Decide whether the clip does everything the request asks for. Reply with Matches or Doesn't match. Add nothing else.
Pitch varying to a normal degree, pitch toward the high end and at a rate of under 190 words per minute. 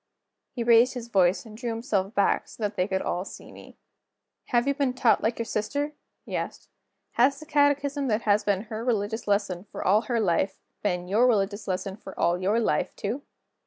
Doesn't match